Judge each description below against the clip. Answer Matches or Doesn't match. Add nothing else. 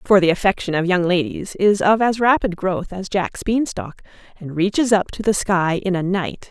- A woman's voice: Matches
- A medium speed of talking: Doesn't match